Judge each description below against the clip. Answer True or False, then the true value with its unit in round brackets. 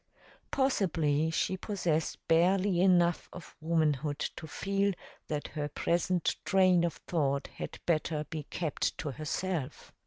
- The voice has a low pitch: False (165 Hz)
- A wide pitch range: False (3.4 semitones)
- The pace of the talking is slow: True (125 wpm)